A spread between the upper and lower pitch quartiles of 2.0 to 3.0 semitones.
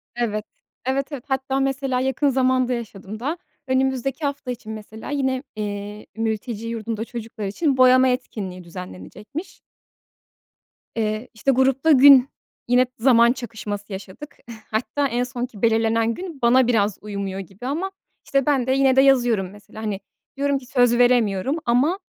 No: average, 3.7 semitones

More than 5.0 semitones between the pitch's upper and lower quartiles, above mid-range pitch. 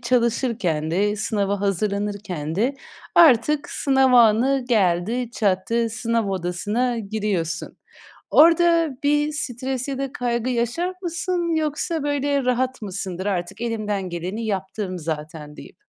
Yes: wide, 5.5 semitones; high, 230 Hz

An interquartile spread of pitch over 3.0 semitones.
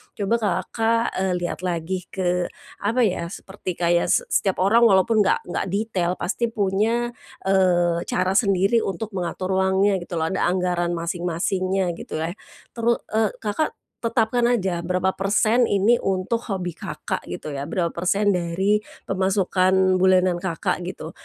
No: average, 2.7 semitones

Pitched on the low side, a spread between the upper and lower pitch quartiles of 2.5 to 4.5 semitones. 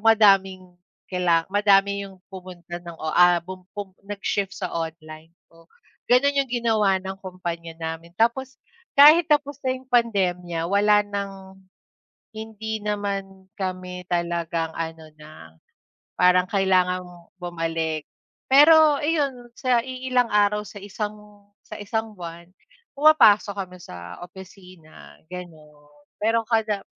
No: high, 195 Hz; average, 4.1 semitones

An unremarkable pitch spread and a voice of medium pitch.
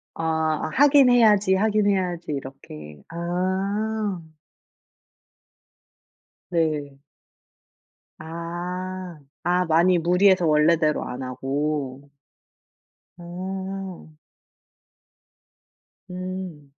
Yes: average, 3.6 semitones; medium, 175 Hz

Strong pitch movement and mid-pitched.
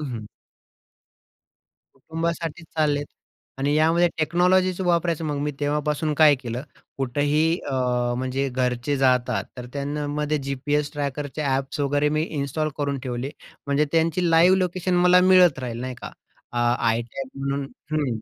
No: average, 3.3 semitones; medium, 145 Hz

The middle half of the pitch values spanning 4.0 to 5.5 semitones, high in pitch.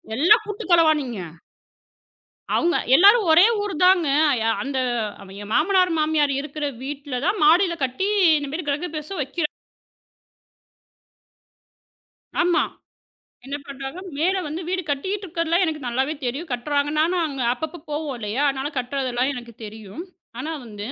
Yes: average, 4.4 semitones; very high, 300 Hz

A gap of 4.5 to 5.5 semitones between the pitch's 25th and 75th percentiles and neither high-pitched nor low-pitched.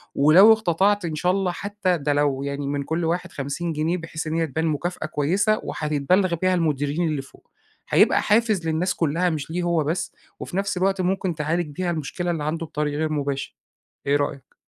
No: average, 3.6 semitones; medium, 165 Hz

